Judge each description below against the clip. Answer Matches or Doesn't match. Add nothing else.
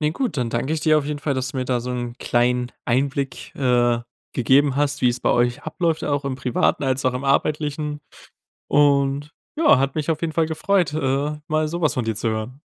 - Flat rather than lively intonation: Doesn't match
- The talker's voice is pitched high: Doesn't match